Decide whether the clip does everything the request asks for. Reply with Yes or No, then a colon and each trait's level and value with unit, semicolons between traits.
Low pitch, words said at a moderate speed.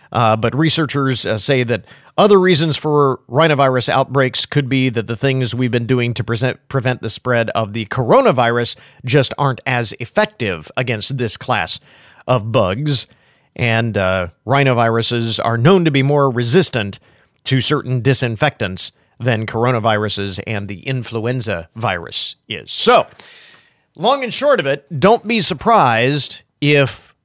Yes: low, 130 Hz; average, 145 wpm